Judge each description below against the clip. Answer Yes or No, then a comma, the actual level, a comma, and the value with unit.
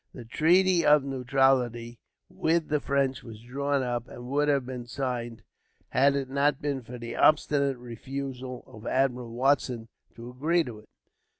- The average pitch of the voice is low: Yes, low, 130 Hz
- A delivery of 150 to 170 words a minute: Yes, average, 160 wpm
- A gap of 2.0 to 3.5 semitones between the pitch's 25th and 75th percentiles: Yes, narrow, 2.6 semitones